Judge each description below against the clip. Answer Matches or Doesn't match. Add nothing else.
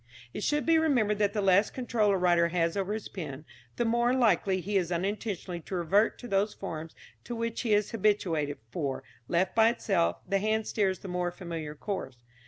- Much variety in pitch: Doesn't match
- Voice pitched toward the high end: Matches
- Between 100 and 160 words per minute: Doesn't match